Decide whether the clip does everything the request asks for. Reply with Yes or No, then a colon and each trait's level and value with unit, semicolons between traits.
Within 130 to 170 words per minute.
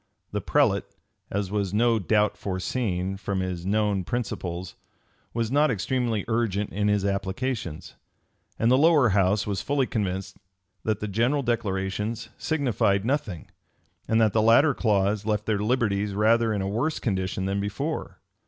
Yes: average, 150 wpm